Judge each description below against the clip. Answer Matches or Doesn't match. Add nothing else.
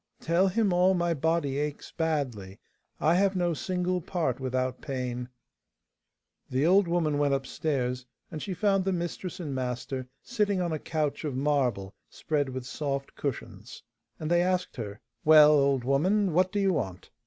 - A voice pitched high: Doesn't match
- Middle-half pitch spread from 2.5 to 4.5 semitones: Doesn't match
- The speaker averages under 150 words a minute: Doesn't match